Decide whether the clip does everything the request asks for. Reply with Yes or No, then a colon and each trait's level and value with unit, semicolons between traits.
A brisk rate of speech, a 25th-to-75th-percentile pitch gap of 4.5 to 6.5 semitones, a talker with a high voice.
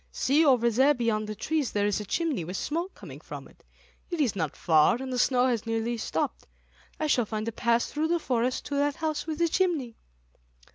Yes: fast, 220 wpm; average, 5.2 semitones; very high, 250 Hz